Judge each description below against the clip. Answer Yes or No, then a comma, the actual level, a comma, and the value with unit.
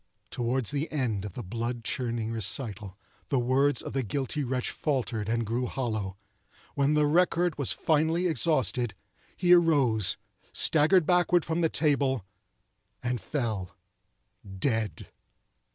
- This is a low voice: Yes, low, 130 Hz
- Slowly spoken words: Yes, slow, 125 wpm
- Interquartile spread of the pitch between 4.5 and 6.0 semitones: Yes, average, 5.2 semitones